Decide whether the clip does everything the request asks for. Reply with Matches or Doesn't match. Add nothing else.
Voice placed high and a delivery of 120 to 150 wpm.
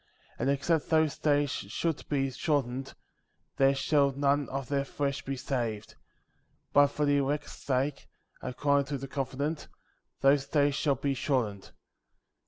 Doesn't match